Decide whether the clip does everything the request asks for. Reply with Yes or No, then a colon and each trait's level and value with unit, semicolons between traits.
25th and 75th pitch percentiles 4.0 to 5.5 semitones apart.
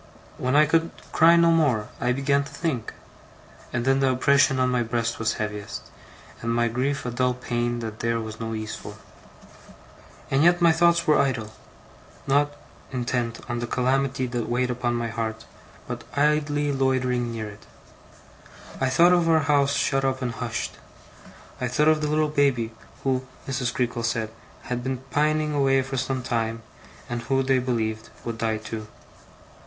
No: average, 3.3 semitones